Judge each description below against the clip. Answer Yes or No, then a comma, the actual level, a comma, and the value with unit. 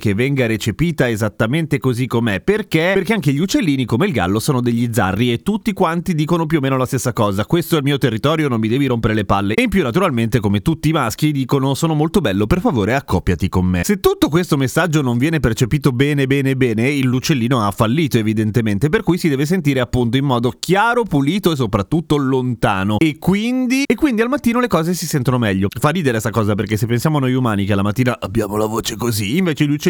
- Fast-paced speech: Yes, fast, 230 wpm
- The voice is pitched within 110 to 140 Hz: Yes, low, 135 Hz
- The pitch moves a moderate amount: No, wide, 5.9 semitones